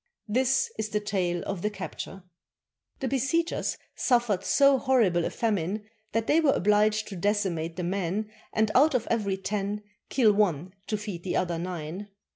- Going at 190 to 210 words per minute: No, average, 170 wpm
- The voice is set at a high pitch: Yes, high, 210 Hz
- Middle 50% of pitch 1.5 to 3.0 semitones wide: No, average, 3.9 semitones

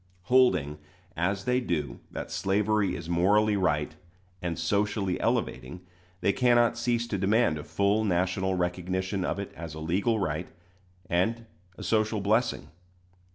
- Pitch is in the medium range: No, very low, 95 Hz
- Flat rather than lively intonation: No, average, 3.7 semitones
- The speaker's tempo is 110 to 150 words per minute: Yes, average, 140 wpm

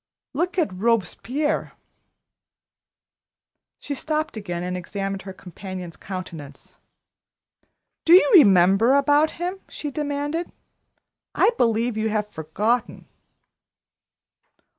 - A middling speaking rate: No, slow, 95 wpm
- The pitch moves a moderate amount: No, wide, 7.7 semitones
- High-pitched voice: Yes, high, 220 Hz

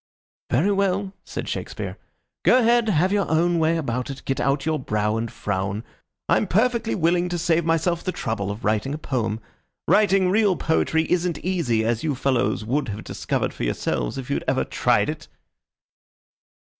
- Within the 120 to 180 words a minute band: Yes, average, 170 wpm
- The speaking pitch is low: No, medium, 160 Hz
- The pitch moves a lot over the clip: Yes, wide, 7.7 semitones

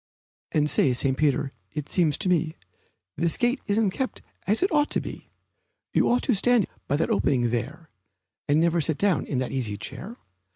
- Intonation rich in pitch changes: Yes, wide, 6.9 semitones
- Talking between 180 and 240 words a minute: Yes, average, 190 wpm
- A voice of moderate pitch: Yes, medium, 160 Hz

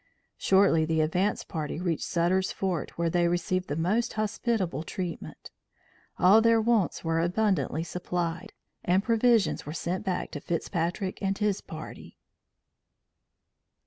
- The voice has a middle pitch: Yes, medium, 180 Hz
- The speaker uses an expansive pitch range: No, average, 3.3 semitones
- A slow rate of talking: Yes, slow, 130 wpm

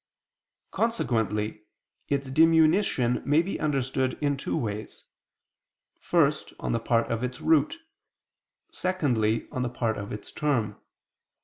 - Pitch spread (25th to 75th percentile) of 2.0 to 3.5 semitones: No, average, 5.1 semitones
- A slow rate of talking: Yes, slow, 120 wpm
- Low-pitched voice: Yes, low, 130 Hz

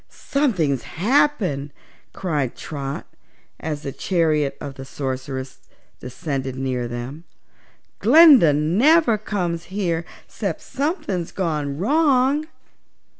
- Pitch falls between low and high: Yes, medium, 165 Hz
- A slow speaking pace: Yes, slow, 95 wpm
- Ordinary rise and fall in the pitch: No, wide, 8.4 semitones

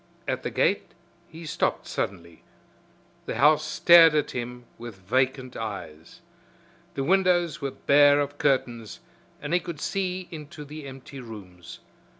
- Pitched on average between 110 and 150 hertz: Yes, medium, 140 Hz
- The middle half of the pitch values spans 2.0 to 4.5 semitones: No, average, 4.9 semitones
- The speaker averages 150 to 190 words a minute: No, average, 140 wpm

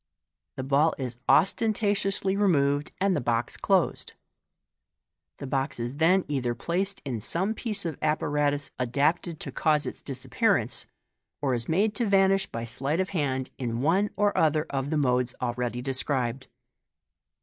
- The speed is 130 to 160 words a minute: Yes, average, 155 wpm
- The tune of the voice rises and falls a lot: Yes, wide, 6.7 semitones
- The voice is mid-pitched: Yes, medium, 145 Hz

